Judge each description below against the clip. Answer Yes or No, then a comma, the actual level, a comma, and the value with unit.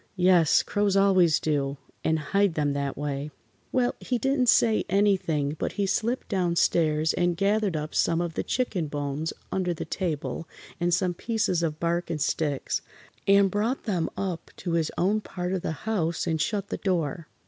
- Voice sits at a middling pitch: Yes, medium, 175 Hz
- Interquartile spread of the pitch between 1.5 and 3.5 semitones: No, average, 4.1 semitones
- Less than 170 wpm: No, average, 180 wpm